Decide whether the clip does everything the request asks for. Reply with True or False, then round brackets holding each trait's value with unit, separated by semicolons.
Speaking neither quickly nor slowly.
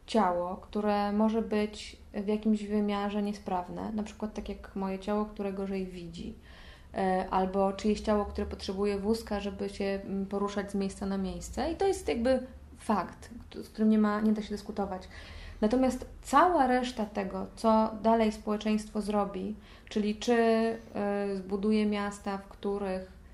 True (145 wpm)